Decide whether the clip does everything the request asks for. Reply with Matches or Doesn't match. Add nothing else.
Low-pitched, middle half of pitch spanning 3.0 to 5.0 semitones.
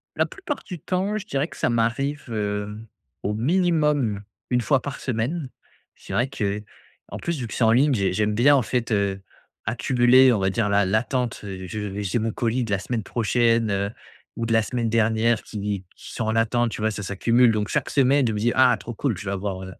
Matches